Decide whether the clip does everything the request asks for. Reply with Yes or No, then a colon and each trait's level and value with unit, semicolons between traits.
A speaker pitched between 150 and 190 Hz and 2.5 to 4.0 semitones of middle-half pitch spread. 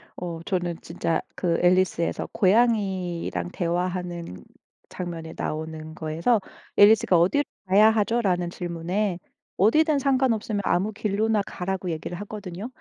Yes: medium, 185 Hz; average, 3.7 semitones